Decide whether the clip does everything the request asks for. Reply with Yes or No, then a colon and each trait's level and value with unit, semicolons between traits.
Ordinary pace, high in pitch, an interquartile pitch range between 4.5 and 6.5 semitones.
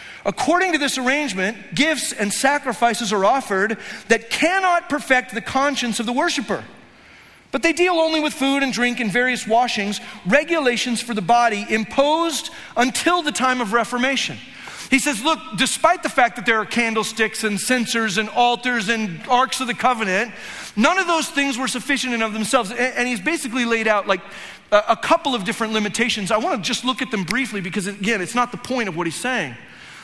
No: average, 190 wpm; high, 245 Hz; average, 3.8 semitones